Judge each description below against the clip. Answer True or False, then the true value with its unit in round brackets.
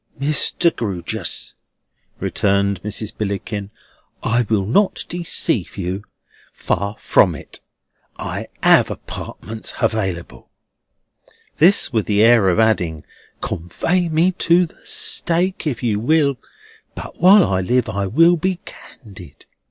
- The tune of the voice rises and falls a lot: True (8.5 semitones)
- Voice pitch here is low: True (110 Hz)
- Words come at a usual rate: False (120 wpm)